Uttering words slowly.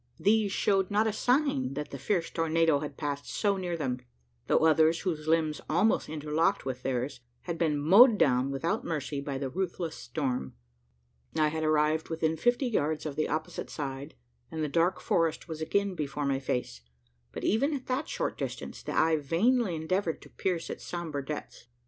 No: average, 180 wpm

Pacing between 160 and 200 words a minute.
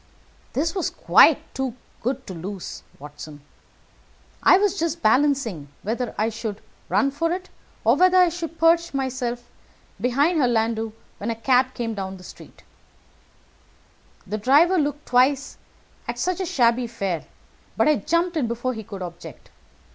No: average, 150 wpm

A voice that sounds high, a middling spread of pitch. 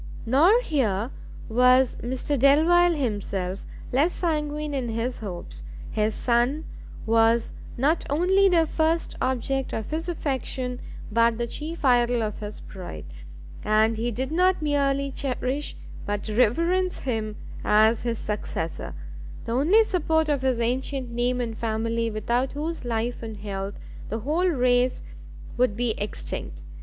Yes: very high, 250 Hz; average, 4.9 semitones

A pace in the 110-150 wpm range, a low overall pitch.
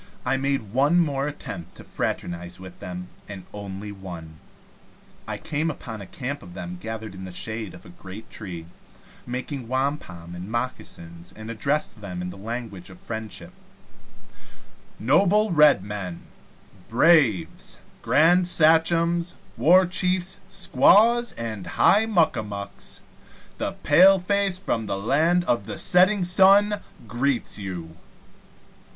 Yes: slow, 135 wpm; low, 120 Hz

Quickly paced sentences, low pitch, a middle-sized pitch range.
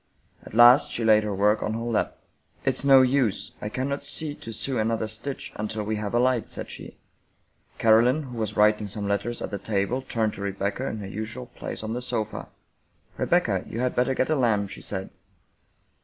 Yes: fast, 210 wpm; low, 110 Hz; average, 3.2 semitones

